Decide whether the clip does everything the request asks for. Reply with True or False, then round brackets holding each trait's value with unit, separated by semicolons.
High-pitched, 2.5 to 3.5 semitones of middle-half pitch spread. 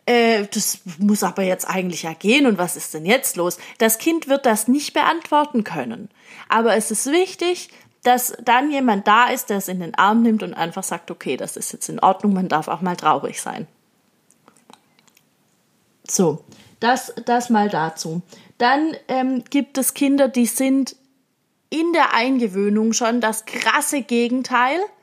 False (230 Hz; 4.5 semitones)